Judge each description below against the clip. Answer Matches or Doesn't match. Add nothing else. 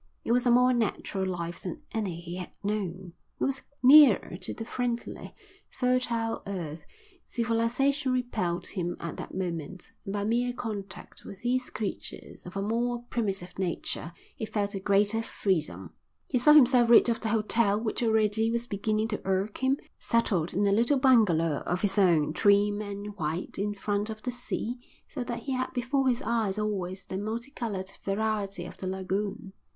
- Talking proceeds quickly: Doesn't match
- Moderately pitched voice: Doesn't match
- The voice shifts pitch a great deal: Doesn't match